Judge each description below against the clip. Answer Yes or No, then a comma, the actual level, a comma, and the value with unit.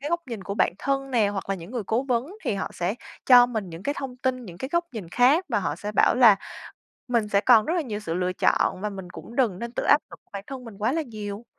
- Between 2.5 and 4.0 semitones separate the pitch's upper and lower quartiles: No, average, 4.5 semitones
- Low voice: No, high, 230 Hz